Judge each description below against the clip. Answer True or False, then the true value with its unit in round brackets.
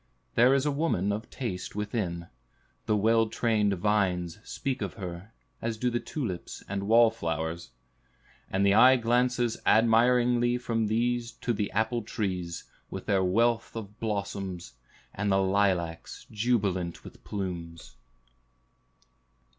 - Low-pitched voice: True (105 Hz)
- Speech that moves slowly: True (130 wpm)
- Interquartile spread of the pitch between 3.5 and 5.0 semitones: True (4.0 semitones)